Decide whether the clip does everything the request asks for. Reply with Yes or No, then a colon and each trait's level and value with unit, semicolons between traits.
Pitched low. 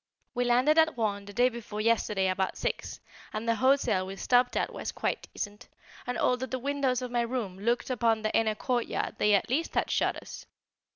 No: high, 235 Hz